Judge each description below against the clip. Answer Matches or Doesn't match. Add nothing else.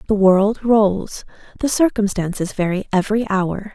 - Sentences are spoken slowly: Matches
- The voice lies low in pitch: Doesn't match